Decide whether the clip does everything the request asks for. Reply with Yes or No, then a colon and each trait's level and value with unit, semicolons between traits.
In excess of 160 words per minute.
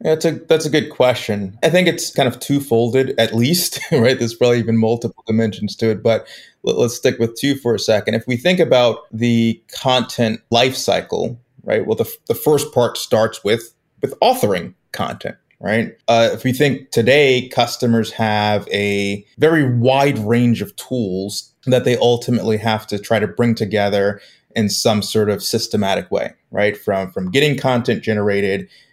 Yes: average, 180 wpm